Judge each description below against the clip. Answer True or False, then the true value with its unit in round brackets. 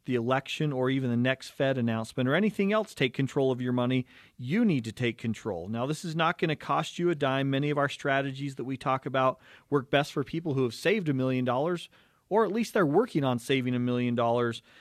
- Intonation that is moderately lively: True (3.7 semitones)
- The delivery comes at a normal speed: False (240 wpm)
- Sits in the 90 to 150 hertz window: True (135 Hz)